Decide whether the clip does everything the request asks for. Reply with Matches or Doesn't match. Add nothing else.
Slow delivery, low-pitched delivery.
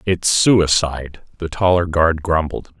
Matches